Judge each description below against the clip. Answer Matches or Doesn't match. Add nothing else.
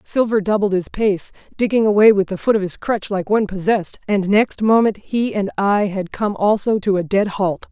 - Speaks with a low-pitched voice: Doesn't match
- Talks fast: Matches